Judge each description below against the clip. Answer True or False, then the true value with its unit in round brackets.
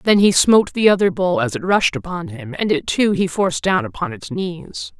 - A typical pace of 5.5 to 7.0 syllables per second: False (5.2 syllables/s)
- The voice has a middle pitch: False (195 Hz)